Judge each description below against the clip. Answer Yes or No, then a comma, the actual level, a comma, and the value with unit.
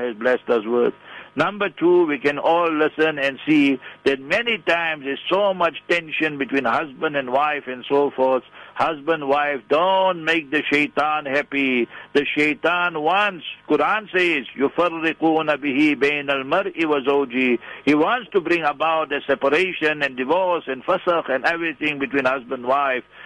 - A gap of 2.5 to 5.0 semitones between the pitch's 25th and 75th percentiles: Yes, average, 3.2 semitones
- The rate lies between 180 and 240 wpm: No, average, 150 wpm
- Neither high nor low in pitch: Yes, medium, 150 Hz